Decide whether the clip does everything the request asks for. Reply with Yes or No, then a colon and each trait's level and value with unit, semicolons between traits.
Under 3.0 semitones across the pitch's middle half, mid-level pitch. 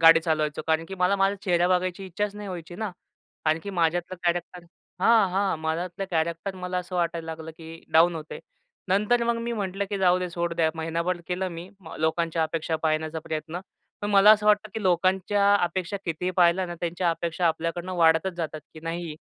Yes: narrow, 2.5 semitones; medium, 175 Hz